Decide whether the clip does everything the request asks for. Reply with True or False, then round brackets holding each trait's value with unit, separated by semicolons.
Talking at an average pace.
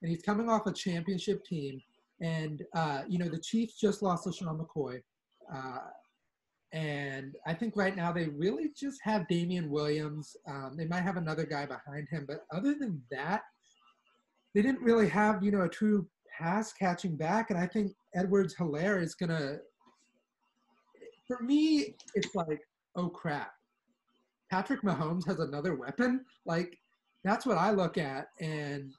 True (165 wpm)